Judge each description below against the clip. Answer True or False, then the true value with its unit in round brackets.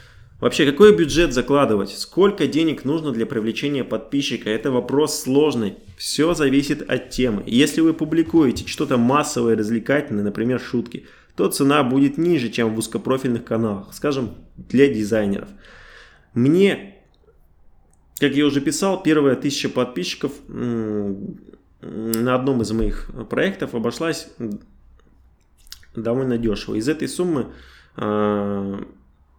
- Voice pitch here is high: False (120 Hz)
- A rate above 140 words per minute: False (110 wpm)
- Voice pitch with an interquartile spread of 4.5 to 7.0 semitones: True (5.4 semitones)